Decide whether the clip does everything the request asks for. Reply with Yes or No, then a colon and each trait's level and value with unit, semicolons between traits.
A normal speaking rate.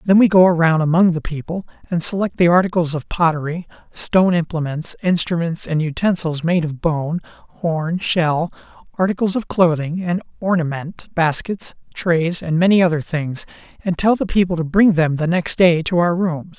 Yes: average, 170 wpm